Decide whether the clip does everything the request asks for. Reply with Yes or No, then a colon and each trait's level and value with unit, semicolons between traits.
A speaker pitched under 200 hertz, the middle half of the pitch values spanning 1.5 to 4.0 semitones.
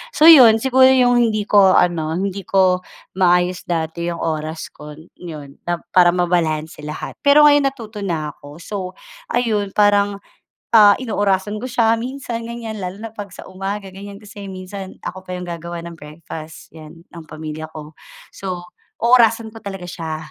No: high, 190 Hz; average, 4.6 semitones